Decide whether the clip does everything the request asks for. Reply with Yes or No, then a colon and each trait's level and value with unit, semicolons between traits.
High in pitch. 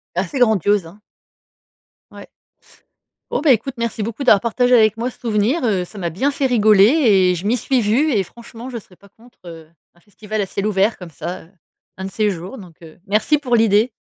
Yes: high, 215 Hz